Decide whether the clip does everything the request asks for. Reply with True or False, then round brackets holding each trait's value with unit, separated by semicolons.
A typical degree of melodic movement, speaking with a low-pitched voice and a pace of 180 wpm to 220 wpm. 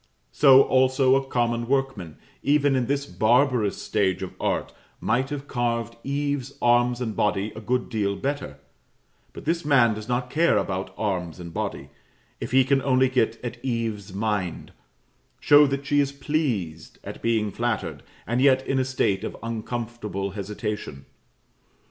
False (4.2 semitones; 120 Hz; 155 wpm)